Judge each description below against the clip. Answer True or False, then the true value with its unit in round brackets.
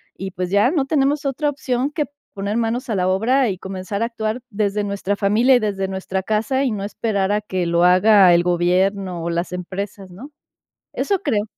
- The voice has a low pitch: False (205 Hz)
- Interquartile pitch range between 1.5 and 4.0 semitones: False (4.5 semitones)